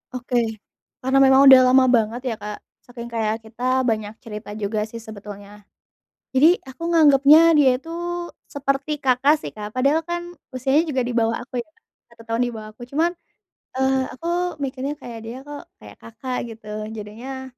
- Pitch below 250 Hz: No, very high, 255 Hz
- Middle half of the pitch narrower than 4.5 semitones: Yes, average, 3.6 semitones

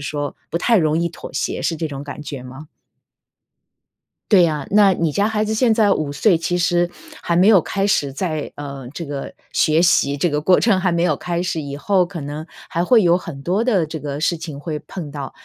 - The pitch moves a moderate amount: Yes, average, 4.1 semitones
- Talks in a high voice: No, medium, 170 Hz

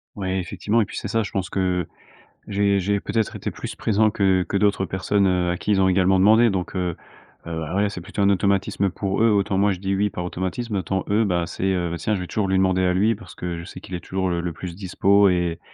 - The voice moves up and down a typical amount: No, narrow, 2.0 semitones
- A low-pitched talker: Yes, very low, 95 Hz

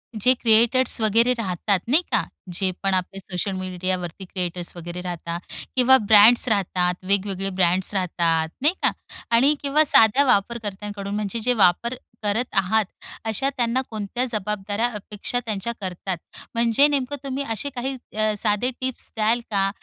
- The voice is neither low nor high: No, high, 210 Hz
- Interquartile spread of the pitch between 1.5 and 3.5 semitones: No, average, 4.2 semitones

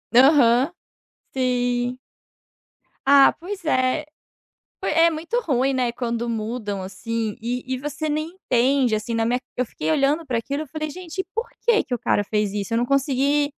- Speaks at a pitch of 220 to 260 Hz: Yes, very high, 255 Hz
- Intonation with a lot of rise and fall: No, average, 4.2 semitones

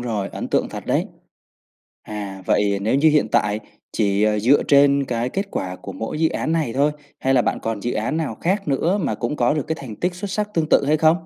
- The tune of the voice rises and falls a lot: Yes, wide, 6.6 semitones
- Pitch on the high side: No, low, 135 Hz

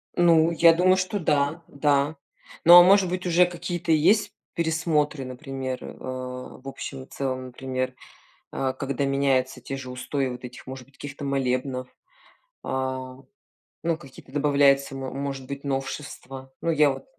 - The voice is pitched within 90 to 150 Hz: Yes, medium, 140 Hz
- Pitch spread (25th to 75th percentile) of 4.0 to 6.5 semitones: No, average, 3.6 semitones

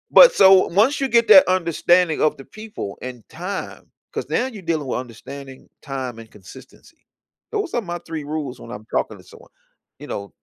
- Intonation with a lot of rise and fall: Yes, wide, 7.7 semitones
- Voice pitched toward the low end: No, medium, 160 Hz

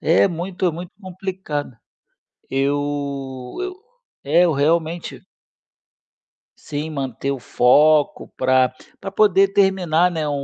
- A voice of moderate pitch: Yes, medium, 160 Hz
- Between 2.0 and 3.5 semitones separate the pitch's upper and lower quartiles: No, average, 4.4 semitones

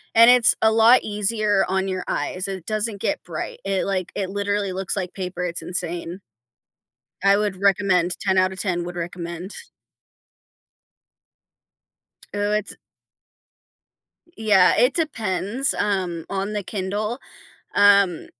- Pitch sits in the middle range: No, high, 195 Hz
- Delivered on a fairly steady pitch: Yes, narrow, 2.3 semitones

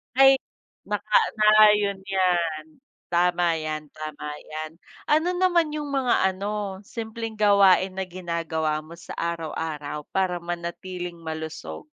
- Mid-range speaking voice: Yes, medium, 180 Hz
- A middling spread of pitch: Yes, average, 4.6 semitones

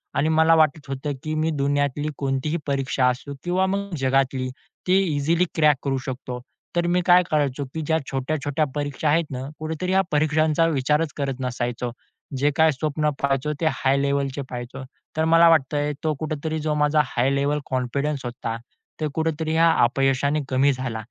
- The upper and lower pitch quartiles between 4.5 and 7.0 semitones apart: No, average, 2.9 semitones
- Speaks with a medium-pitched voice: Yes, medium, 145 Hz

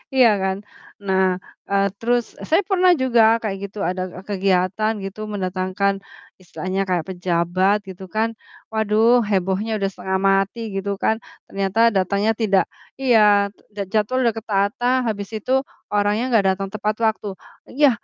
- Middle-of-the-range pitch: No, high, 200 Hz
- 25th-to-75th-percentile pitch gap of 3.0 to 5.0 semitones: No, narrow, 2.6 semitones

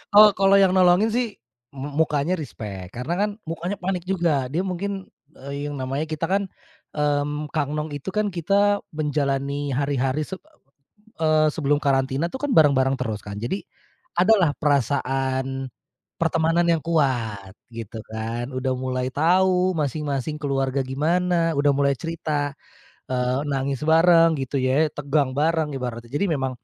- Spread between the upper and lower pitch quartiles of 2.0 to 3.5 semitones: No, average, 4.0 semitones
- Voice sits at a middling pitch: Yes, medium, 145 Hz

